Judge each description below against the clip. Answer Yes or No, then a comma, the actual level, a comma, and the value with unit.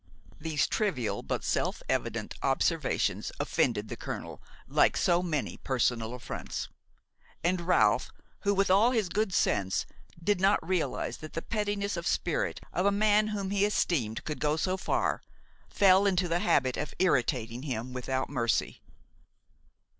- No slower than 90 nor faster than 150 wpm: Yes, average, 145 wpm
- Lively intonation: Yes, wide, 7.2 semitones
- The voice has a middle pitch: Yes, medium, 175 Hz